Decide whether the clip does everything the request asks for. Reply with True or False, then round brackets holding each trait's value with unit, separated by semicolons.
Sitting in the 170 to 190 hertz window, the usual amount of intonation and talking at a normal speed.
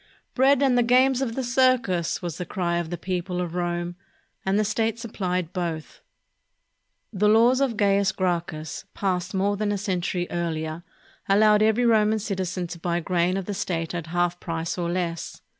True (185 Hz; 3.8 semitones; 175 wpm)